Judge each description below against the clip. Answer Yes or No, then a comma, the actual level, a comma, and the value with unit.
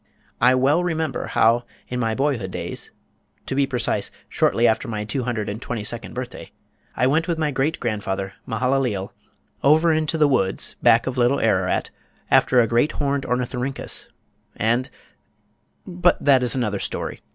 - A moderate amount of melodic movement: Yes, average, 3.7 semitones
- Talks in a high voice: No, low, 125 Hz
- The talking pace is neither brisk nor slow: Yes, average, 160 wpm